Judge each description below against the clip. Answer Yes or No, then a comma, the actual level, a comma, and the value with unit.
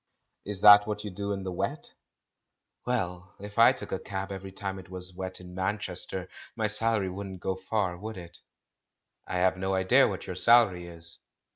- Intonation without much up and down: Yes, narrow, 2.1 semitones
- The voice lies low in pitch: Yes, very low, 95 Hz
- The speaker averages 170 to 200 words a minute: Yes, average, 185 wpm